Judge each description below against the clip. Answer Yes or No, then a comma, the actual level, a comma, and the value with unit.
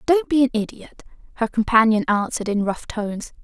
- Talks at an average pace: Yes, average, 175 wpm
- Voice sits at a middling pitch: No, high, 230 Hz